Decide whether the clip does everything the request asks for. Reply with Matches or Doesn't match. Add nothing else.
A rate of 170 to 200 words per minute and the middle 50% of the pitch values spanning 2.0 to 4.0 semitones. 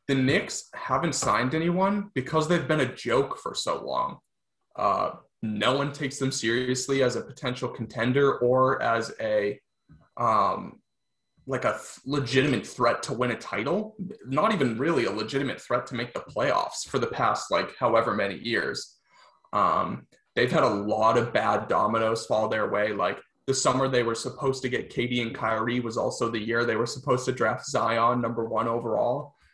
Matches